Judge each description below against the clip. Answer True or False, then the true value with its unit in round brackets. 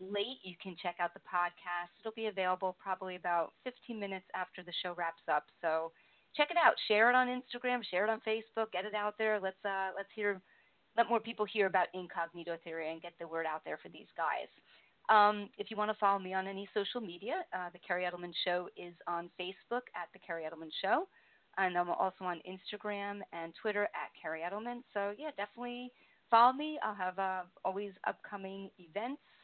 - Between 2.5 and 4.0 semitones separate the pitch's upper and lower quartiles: True (3.5 semitones)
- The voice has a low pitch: False (195 Hz)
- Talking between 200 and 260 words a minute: True (205 wpm)